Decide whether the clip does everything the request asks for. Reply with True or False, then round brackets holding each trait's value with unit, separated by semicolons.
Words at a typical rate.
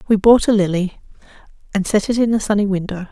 False (210 wpm)